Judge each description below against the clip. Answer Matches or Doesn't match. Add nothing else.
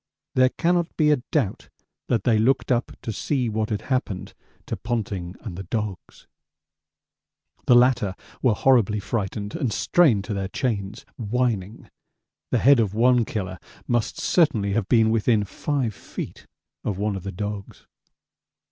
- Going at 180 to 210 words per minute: Doesn't match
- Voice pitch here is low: Matches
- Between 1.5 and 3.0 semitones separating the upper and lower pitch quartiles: Doesn't match